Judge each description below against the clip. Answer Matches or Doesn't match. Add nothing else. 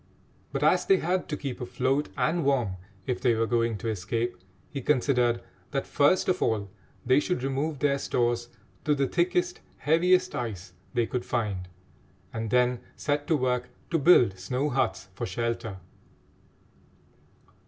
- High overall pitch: Doesn't match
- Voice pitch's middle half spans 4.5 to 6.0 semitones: Doesn't match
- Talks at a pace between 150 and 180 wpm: Matches